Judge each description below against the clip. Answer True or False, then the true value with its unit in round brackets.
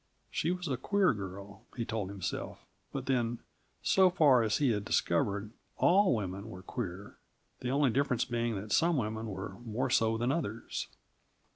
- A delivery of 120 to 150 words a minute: False (165 wpm)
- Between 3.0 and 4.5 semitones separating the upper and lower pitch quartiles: False (4.9 semitones)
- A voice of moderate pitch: False (115 Hz)